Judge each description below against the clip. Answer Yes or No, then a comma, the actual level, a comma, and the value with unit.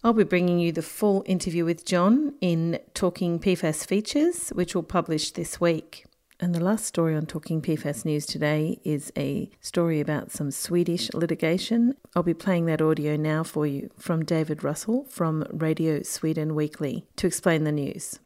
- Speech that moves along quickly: No, average, 175 wpm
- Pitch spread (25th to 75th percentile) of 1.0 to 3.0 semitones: Yes, average, 2.7 semitones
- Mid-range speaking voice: Yes, medium, 170 Hz